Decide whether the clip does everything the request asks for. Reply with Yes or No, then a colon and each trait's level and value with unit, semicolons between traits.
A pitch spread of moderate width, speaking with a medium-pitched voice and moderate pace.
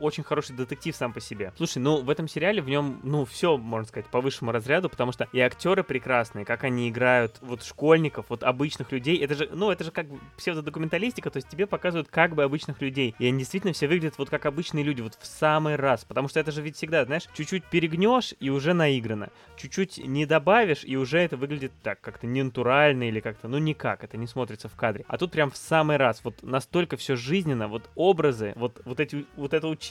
No: average, 4.1 semitones; medium, 145 Hz; fast, 225 wpm